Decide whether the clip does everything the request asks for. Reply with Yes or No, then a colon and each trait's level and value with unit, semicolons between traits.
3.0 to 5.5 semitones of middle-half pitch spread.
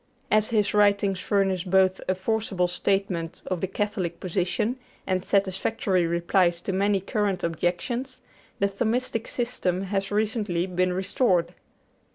No: narrow, 2.4 semitones